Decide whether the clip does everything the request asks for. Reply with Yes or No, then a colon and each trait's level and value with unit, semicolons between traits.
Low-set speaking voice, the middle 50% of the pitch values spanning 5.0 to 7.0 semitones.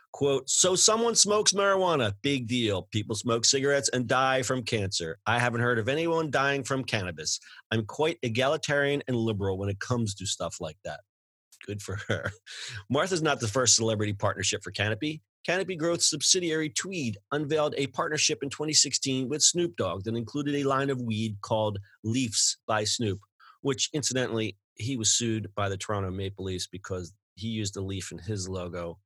Yes: low, 120 Hz; wide, 5.5 semitones